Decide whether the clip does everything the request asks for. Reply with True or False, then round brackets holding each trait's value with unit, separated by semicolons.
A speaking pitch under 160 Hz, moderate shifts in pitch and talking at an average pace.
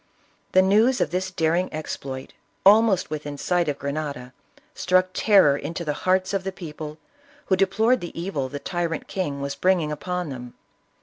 False (175 Hz; 4.2 semitones; 165 wpm)